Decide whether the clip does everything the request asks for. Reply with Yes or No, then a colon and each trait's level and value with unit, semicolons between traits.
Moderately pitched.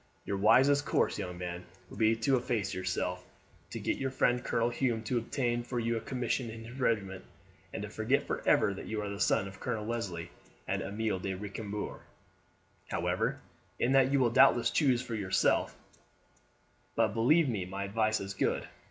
No: low, 115 Hz